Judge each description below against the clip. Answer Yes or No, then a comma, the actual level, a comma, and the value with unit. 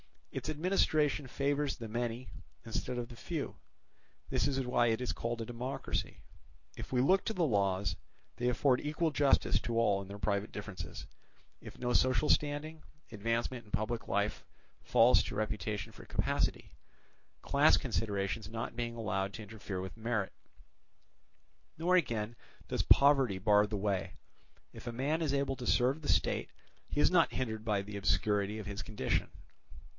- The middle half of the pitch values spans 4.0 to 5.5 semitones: Yes, average, 4.8 semitones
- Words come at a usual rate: Yes, average, 160 wpm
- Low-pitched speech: Yes, low, 115 Hz